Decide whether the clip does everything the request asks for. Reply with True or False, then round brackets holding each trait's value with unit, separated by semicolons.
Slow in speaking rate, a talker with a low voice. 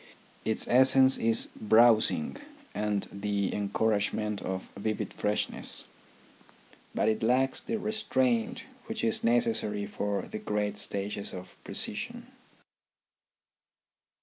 True (100 wpm; 110 Hz)